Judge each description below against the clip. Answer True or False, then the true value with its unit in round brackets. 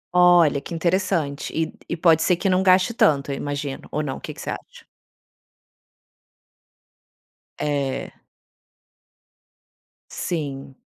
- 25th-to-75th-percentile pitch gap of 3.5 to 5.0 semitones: True (4.0 semitones)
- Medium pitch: True (160 Hz)